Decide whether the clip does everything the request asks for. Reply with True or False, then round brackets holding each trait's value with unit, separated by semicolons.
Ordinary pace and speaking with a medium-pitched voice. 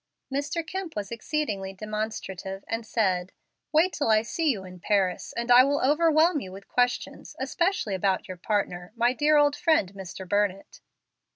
False (165 wpm; 220 Hz)